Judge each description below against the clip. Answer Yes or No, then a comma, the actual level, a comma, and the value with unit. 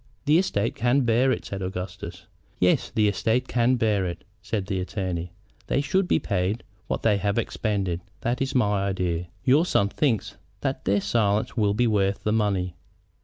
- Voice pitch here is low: Yes, low, 105 Hz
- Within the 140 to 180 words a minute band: Yes, average, 175 wpm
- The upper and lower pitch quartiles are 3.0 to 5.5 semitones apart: Yes, average, 3.9 semitones